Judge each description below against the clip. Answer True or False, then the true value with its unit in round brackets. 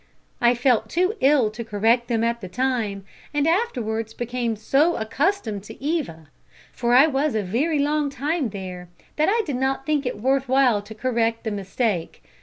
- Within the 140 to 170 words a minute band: False (180 wpm)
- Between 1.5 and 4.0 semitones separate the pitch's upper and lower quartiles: False (4.5 semitones)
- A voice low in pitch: False (245 Hz)